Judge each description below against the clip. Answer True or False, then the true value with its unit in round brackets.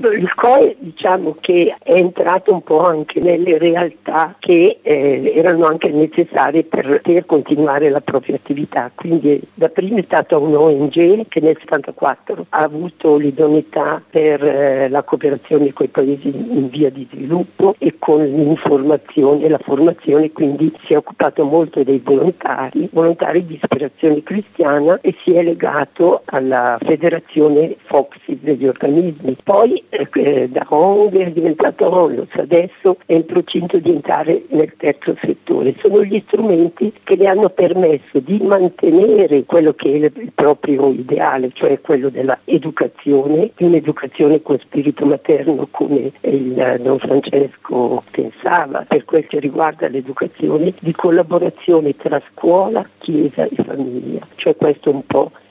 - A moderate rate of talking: True (145 wpm)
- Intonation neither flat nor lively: True (3.5 semitones)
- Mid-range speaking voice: True (155 Hz)